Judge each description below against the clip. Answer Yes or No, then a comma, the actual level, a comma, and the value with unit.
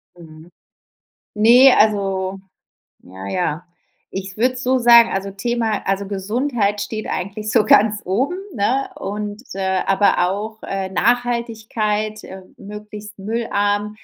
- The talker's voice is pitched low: No, high, 210 Hz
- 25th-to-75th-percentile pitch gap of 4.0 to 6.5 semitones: No, average, 2.8 semitones